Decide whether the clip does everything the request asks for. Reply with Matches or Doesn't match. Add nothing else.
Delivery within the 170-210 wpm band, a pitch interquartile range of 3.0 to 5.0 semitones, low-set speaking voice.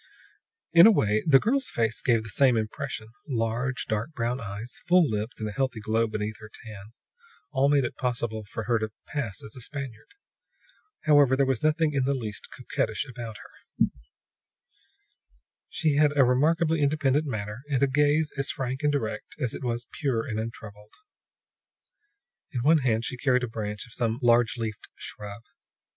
Matches